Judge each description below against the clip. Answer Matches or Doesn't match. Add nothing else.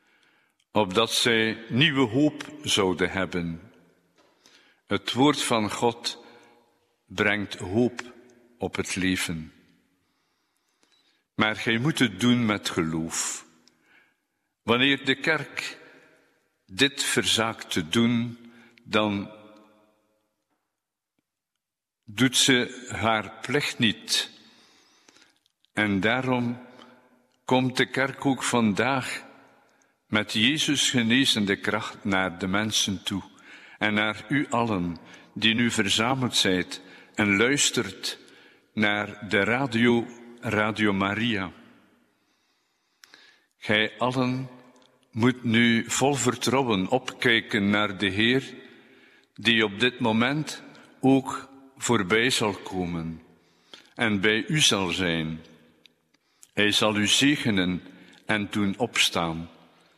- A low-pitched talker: Matches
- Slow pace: Matches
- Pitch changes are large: Doesn't match